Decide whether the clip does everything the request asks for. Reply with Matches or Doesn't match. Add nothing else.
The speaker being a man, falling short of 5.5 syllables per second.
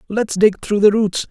Matches